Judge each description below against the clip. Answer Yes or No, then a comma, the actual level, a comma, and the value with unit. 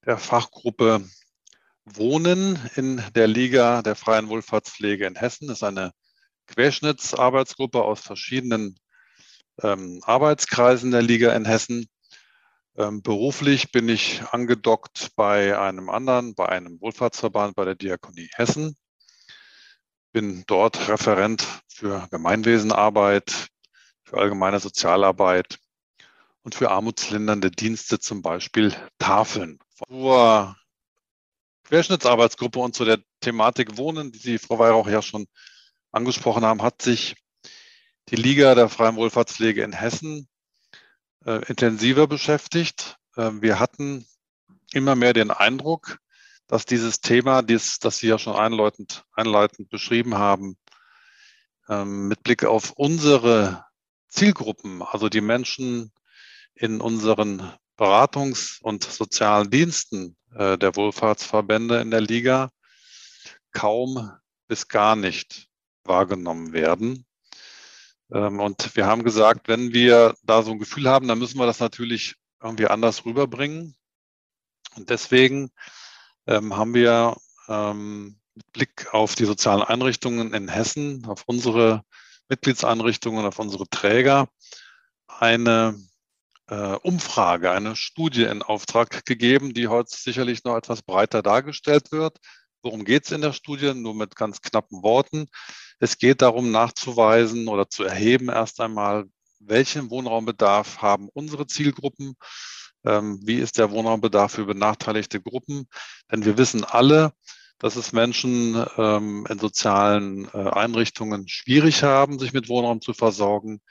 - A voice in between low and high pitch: No, low, 115 Hz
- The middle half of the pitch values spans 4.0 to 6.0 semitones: No, average, 3.5 semitones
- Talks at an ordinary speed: No, slow, 120 wpm